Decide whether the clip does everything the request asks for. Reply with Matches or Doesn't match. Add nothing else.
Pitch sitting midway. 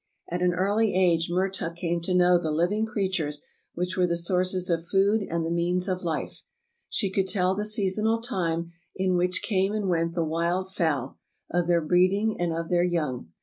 Matches